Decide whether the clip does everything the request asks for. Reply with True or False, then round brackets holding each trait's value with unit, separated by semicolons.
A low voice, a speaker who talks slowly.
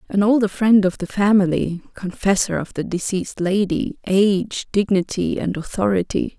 False (195 Hz; 120 wpm)